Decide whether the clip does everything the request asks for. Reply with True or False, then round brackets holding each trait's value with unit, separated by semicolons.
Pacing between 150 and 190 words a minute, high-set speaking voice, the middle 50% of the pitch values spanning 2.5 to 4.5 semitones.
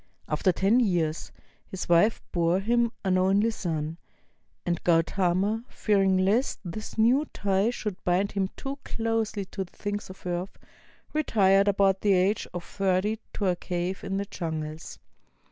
True (155 wpm; 195 Hz; 2.9 semitones)